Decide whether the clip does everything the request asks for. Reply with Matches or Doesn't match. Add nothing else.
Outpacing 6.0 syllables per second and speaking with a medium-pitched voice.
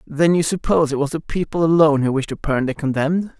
Matches